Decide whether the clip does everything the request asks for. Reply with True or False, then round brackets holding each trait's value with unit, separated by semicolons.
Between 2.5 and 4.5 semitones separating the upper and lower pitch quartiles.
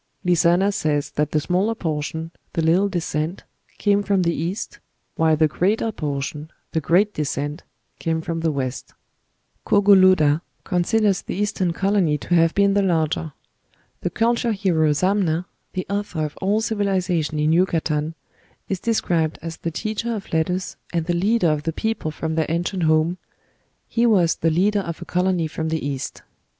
True (3.8 semitones)